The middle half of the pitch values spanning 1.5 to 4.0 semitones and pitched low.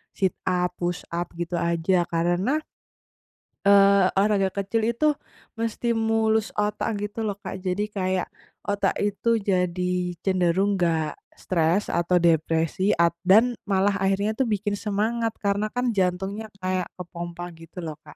No: average, 2.8 semitones; high, 190 Hz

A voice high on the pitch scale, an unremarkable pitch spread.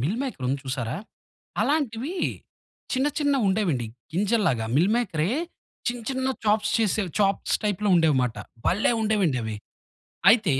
No: high, 205 Hz; wide, 7.7 semitones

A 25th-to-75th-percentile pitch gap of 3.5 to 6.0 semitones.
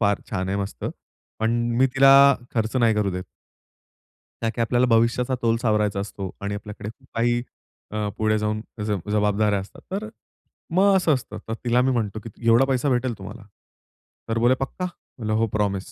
No: average, 2.8 semitones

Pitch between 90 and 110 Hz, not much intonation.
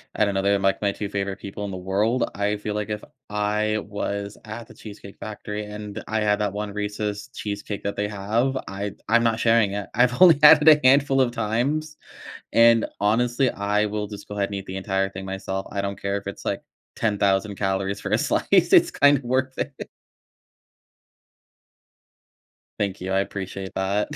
Yes: low, 105 Hz; narrow, 2.3 semitones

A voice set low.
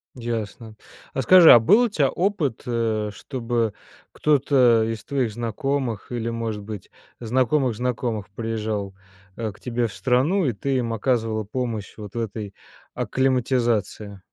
Yes: low, 115 Hz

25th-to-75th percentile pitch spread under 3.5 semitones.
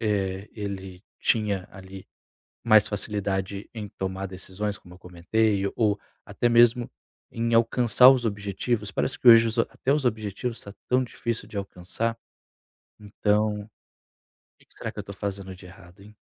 Yes: average, 3.0 semitones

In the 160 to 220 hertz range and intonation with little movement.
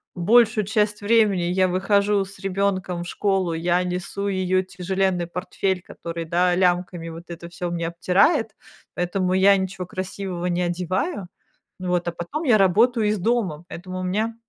Yes: medium, 185 Hz; narrow, 2.2 semitones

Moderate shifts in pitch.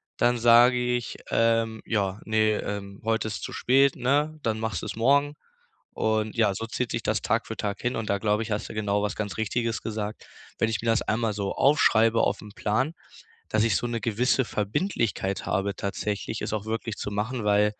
No: narrow, 2.2 semitones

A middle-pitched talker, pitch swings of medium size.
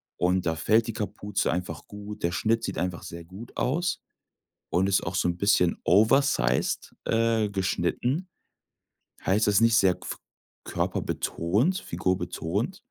No: low, 100 Hz; average, 4.3 semitones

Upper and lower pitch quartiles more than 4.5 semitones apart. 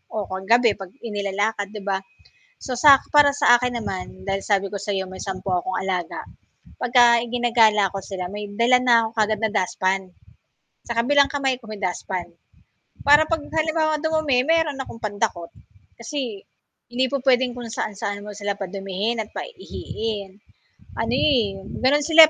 Yes: average, 4.9 semitones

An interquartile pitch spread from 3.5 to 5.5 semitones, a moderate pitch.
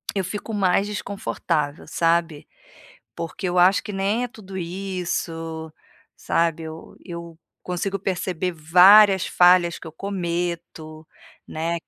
No: average, 2.8 semitones; medium, 175 Hz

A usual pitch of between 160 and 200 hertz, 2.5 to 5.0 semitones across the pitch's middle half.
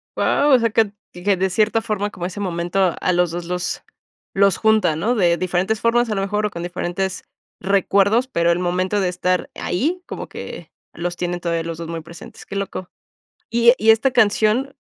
Yes: high, 190 Hz; average, 3.7 semitones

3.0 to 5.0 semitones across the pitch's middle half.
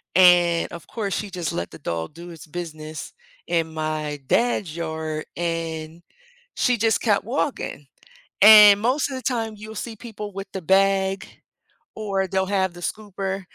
Yes: average, 4.4 semitones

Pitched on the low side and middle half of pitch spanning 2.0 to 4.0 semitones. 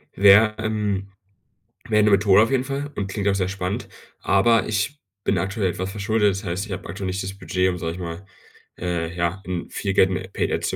Yes: low, 100 Hz; narrow, 2.4 semitones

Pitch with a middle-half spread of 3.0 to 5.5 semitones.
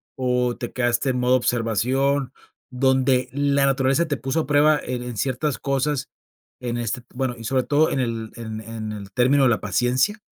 No: narrow, 2.4 semitones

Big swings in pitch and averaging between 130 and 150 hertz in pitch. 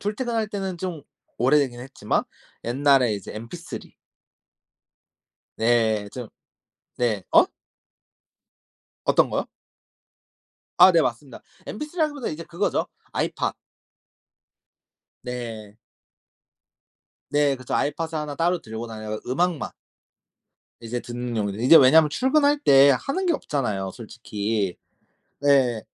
Yes: wide, 6.9 semitones; low, 135 Hz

